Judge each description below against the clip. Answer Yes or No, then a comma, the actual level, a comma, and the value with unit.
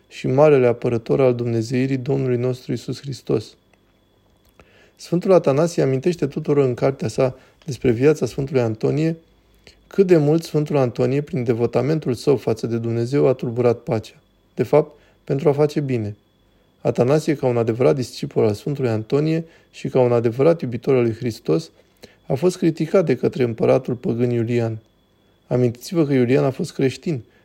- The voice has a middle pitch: No, low, 130 Hz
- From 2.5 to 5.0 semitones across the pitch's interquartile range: Yes, average, 3.9 semitones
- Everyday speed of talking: Yes, average, 155 wpm